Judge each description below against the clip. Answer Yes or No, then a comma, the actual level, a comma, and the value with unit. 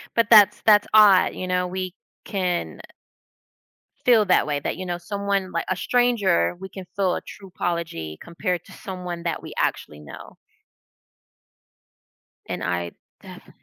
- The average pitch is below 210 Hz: Yes, medium, 185 Hz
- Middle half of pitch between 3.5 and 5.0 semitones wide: No, average, 2.8 semitones